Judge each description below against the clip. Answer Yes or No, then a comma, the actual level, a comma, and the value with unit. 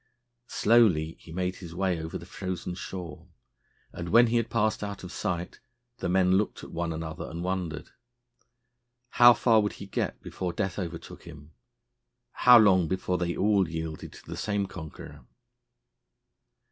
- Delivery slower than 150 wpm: No, average, 160 wpm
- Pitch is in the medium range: No, very low, 90 Hz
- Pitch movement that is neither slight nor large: Yes, average, 3.4 semitones